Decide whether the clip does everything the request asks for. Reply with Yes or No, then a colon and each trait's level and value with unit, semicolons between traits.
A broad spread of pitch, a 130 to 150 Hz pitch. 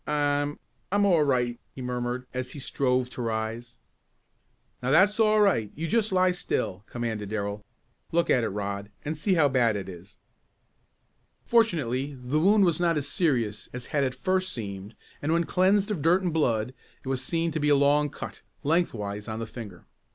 Yes: wide, 6.5 semitones; low, 135 Hz